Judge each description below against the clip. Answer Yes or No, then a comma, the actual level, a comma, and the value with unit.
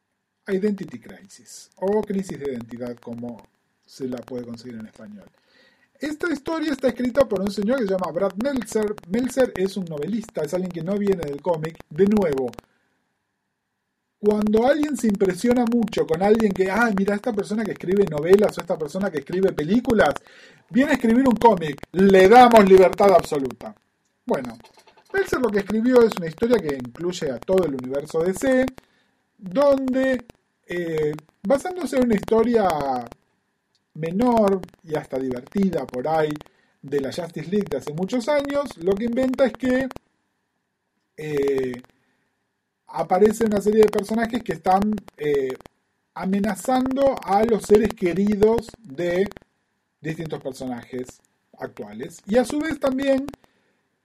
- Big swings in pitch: Yes, wide, 6.6 semitones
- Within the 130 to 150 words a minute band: Yes, average, 145 wpm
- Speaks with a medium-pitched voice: No, high, 200 Hz